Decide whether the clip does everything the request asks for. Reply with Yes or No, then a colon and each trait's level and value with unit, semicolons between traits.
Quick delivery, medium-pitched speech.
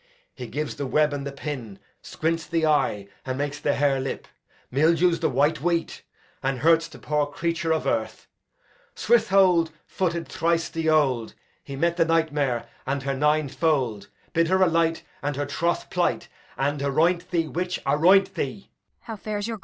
No: average, 160 wpm; medium, 155 Hz